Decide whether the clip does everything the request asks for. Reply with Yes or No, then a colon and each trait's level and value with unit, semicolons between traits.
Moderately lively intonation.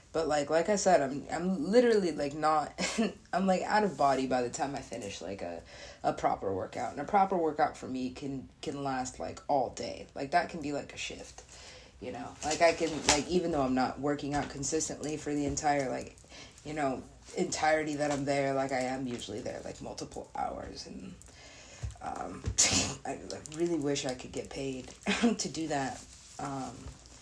Yes: average, 3.4 semitones